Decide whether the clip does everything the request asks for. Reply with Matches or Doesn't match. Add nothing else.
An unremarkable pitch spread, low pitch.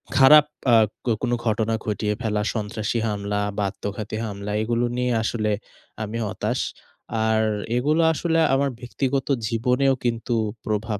Matches